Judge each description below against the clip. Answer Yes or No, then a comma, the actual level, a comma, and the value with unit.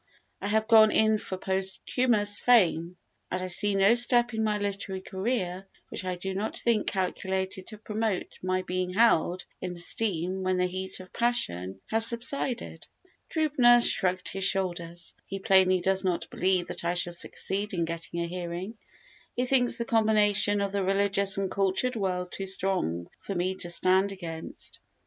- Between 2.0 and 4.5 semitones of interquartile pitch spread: Yes, average, 2.9 semitones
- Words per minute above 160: Yes, average, 170 wpm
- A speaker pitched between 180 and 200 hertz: Yes, high, 190 Hz